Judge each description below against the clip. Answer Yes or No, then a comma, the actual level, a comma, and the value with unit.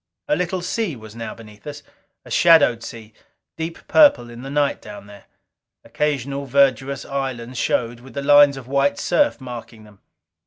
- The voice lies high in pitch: No, low, 135 Hz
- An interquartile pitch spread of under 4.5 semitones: Yes, average, 3.8 semitones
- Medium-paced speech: Yes, average, 165 wpm